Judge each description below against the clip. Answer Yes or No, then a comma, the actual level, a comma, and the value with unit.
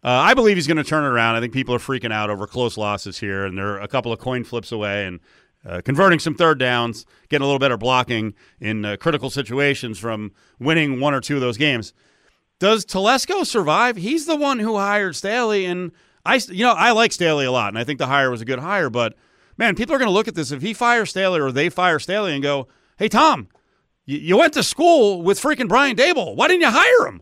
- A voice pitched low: No, medium, 145 Hz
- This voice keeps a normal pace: No, fast, 245 wpm